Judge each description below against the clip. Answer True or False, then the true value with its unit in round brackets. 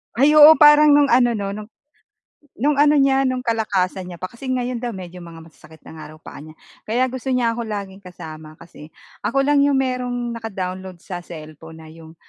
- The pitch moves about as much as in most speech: False (7.3 semitones)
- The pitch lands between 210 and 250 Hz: True (220 Hz)